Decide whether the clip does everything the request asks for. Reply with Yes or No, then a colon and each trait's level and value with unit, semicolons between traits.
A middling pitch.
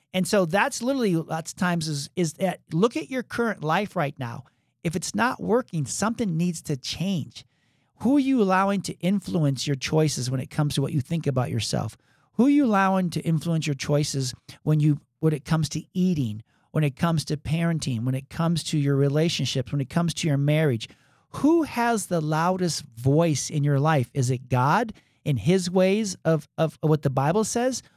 Yes: medium, 160 Hz